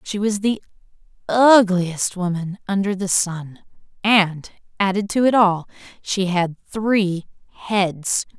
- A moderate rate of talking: No, slow, 120 wpm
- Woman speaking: Yes, female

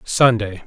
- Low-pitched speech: Yes, low, 110 Hz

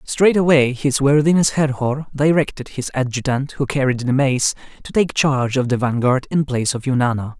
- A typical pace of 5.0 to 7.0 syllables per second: Yes, 5.1 syllables/s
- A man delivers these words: Yes, male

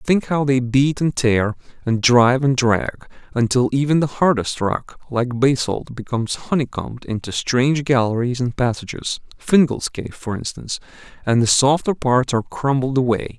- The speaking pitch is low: Yes, low, 130 Hz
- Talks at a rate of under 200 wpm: Yes, average, 150 wpm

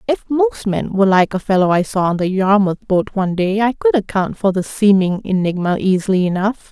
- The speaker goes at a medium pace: No, fast, 215 wpm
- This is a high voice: Yes, high, 200 Hz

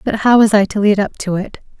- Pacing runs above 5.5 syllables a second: Yes, 5.8 syllables/s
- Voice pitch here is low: No, high, 205 Hz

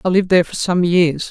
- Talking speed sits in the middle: No, fast, 275 wpm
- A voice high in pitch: No, medium, 175 Hz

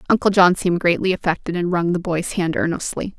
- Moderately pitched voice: Yes, medium, 175 Hz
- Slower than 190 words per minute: No, fast, 205 wpm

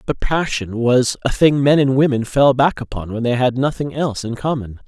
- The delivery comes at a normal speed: No, fast, 220 wpm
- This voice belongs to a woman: No, male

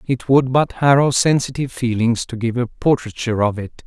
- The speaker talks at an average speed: Yes, average, 185 wpm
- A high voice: No, low, 125 Hz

